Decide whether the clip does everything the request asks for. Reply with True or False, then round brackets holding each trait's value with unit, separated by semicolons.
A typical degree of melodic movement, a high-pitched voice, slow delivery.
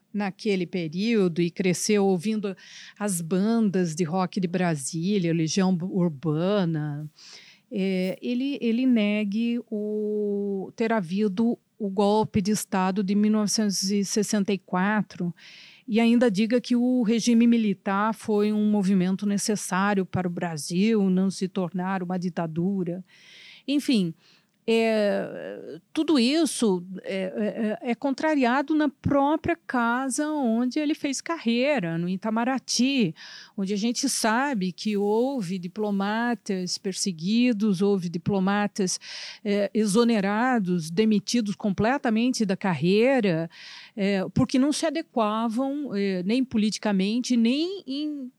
True (3.7 semitones; 210 Hz; 110 wpm)